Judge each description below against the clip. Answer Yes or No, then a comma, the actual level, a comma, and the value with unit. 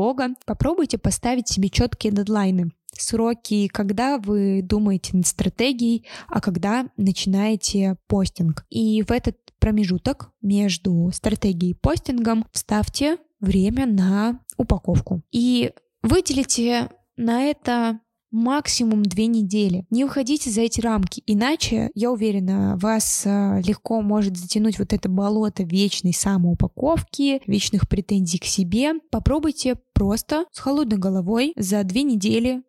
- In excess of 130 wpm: No, average, 115 wpm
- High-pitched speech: Yes, high, 215 Hz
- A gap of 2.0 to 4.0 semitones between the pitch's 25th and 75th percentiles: Yes, average, 3.7 semitones